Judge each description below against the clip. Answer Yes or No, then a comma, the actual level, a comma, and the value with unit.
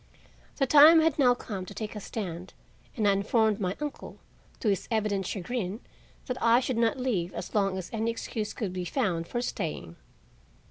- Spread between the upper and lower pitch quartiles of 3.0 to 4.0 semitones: No, average, 4.4 semitones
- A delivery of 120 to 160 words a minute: No, average, 185 wpm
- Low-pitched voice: No, high, 215 Hz